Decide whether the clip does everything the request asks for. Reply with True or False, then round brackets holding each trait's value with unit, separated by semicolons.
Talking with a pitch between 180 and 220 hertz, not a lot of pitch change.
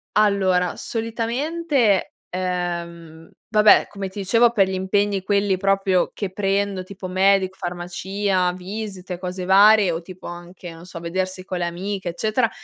True (190 Hz; 2.2 semitones)